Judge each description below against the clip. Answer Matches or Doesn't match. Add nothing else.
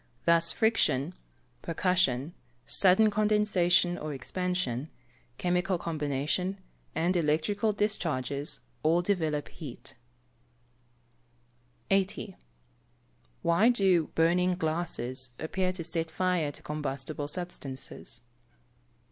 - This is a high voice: Doesn't match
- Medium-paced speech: Doesn't match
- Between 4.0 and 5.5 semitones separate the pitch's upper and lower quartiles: Doesn't match